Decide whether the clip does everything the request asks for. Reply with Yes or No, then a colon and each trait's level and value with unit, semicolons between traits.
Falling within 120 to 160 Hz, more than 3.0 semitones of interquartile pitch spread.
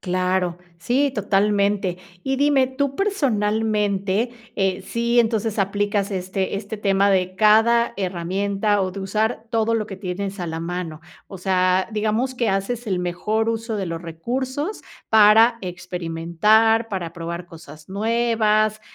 No: high, 205 Hz; average, 3.5 semitones